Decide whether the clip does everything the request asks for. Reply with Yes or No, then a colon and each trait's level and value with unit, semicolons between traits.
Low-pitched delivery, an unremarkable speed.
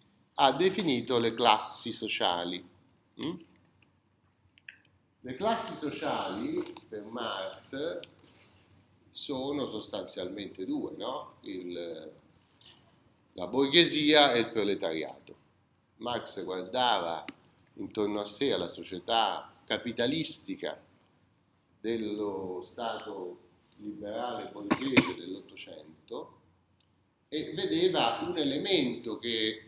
No: low, 115 Hz; slow, 80 wpm